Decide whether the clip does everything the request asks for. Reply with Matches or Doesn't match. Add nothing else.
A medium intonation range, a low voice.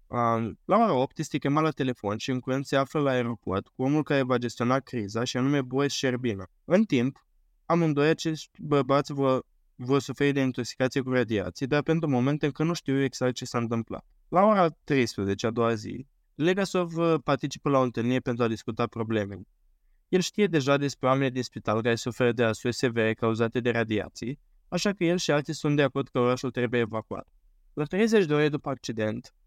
Matches